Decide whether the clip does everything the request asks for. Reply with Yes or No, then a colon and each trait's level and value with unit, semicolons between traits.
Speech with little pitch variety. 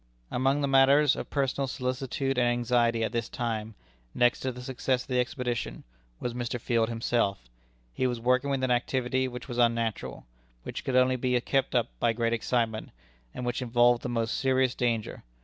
Yes: narrow, 1.8 semitones